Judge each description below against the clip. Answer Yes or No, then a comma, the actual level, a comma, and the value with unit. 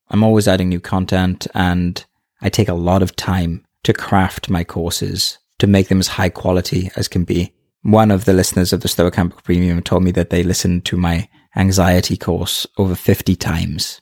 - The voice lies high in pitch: No, very low, 90 Hz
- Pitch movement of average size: No, narrow, 1.4 semitones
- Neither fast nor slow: Yes, average, 195 wpm